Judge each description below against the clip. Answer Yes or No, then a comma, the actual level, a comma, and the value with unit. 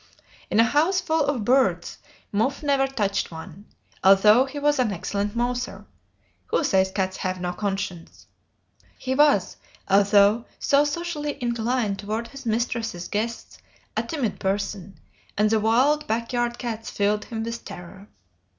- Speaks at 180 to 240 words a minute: No, average, 145 wpm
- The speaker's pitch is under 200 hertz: No, high, 225 Hz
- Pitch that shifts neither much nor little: Yes, average, 4.7 semitones